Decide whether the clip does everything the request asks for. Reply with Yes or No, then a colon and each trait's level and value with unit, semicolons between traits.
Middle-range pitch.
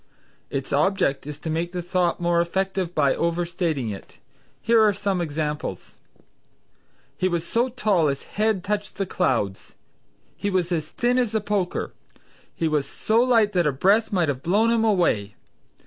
Yes: medium, 180 Hz